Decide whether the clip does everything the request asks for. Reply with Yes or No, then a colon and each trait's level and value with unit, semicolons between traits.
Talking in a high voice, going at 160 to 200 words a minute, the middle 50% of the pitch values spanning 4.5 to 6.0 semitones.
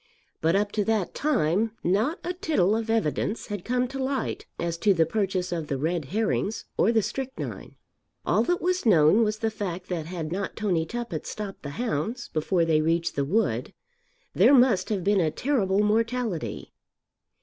Yes: high, 205 Hz; average, 180 wpm; average, 5.2 semitones